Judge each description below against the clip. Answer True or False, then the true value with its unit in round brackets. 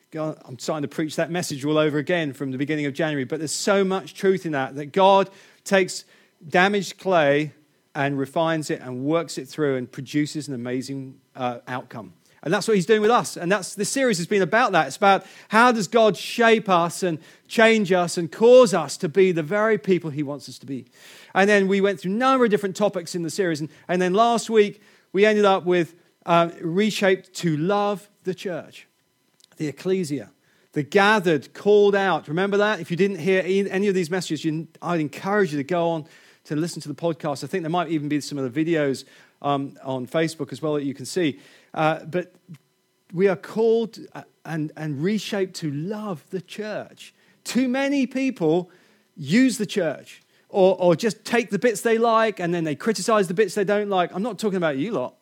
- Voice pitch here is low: False (180 Hz)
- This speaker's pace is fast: True (210 wpm)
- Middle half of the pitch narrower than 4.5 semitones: False (4.8 semitones)